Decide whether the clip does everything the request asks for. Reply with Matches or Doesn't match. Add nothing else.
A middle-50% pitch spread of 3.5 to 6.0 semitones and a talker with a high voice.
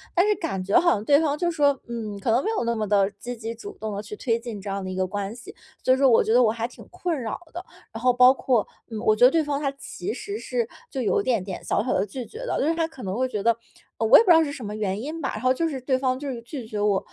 Matches